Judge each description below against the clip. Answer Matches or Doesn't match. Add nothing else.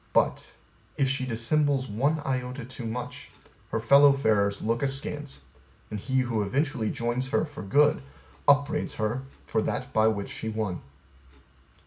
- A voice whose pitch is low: Matches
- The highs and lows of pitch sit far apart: Doesn't match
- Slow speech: Doesn't match